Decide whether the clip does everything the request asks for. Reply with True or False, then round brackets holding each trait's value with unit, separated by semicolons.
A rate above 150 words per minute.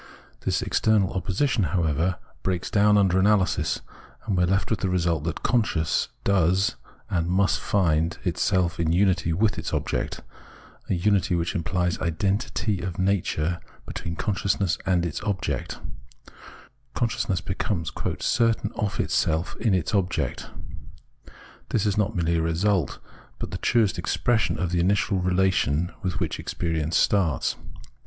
False (140 wpm)